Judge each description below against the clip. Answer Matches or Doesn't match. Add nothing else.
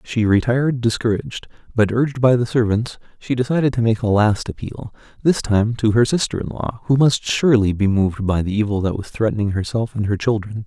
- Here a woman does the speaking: Doesn't match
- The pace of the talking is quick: Matches